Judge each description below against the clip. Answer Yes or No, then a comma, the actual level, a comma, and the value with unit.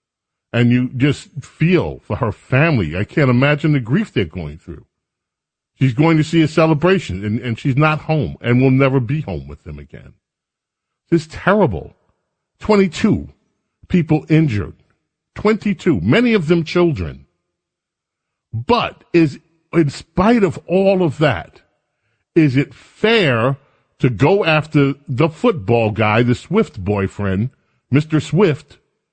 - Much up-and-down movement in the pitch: Yes, wide, 5.8 semitones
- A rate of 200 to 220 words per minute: No, average, 140 wpm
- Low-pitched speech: No, medium, 145 Hz